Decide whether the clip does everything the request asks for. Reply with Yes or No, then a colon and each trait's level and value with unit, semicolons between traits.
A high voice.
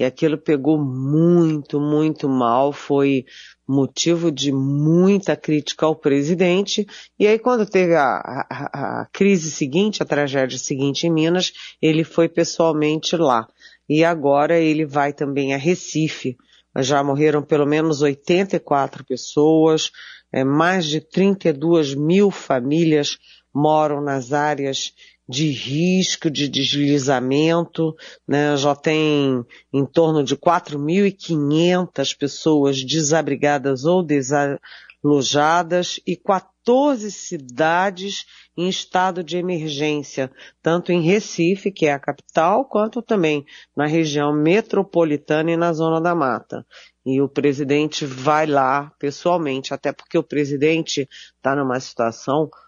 No: medium, 155 Hz